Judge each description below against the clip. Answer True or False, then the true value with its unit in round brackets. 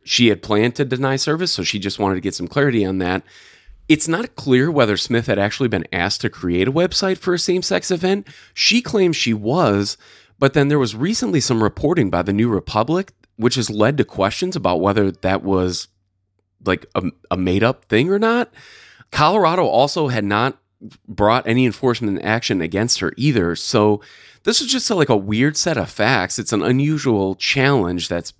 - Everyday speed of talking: True (195 wpm)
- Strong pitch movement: True (6.9 semitones)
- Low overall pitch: True (115 Hz)